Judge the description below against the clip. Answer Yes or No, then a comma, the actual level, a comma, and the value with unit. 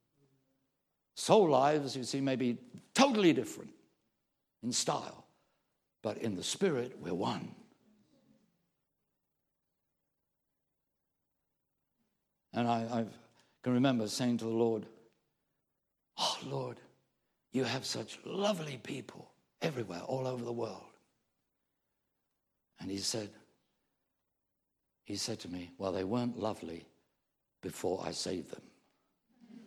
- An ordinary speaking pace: No, slow, 105 wpm